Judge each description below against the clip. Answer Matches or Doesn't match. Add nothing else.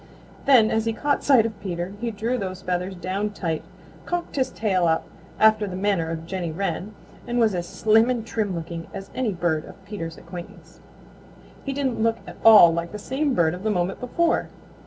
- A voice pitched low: Doesn't match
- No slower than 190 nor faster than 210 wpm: Matches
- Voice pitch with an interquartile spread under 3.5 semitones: Doesn't match